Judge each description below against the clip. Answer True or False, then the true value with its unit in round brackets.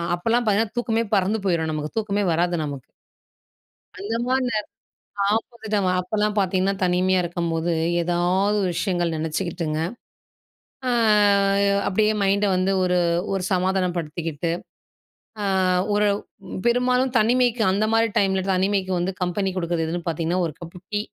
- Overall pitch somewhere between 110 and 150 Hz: False (185 Hz)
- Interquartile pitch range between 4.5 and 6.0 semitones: False (3.4 semitones)